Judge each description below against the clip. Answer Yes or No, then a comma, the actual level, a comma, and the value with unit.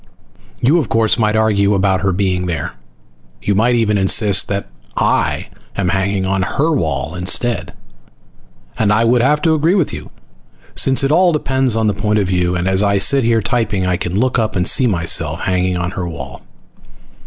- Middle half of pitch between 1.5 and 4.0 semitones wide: No, average, 4.4 semitones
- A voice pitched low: Yes, low, 100 Hz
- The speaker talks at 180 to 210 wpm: Yes, average, 190 wpm